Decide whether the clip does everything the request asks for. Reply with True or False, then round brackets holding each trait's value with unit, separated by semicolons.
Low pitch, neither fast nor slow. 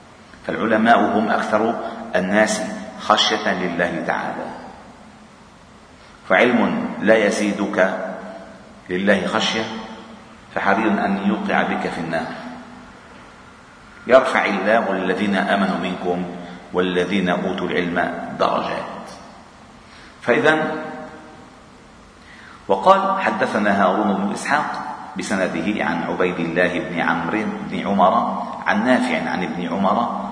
True (95 Hz; 90 wpm)